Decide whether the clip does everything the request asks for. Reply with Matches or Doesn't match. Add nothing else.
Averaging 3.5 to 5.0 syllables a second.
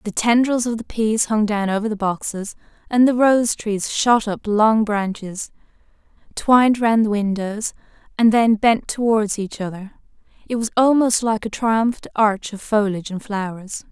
Matches